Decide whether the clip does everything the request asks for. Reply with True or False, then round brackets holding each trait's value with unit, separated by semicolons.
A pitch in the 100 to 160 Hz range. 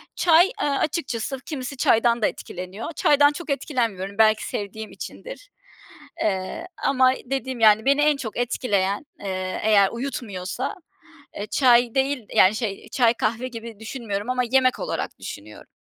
False (235 Hz)